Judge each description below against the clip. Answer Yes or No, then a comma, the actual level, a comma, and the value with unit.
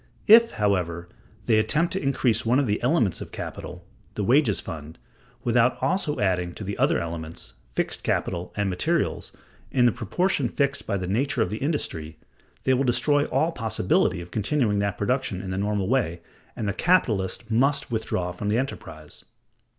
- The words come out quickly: No, average, 175 wpm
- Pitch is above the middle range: No, low, 110 Hz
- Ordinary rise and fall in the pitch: No, wide, 6.4 semitones